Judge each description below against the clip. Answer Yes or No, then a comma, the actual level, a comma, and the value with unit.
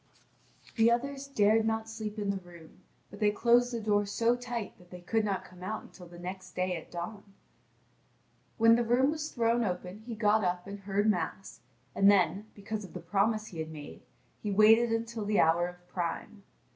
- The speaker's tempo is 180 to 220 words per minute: Yes, average, 195 wpm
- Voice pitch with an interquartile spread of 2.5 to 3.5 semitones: No, average, 3.9 semitones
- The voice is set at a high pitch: Yes, high, 205 Hz